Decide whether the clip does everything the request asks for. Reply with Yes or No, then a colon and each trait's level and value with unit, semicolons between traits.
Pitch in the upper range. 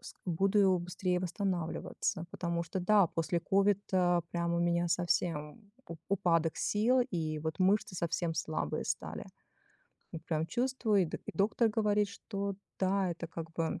No: medium, 180 Hz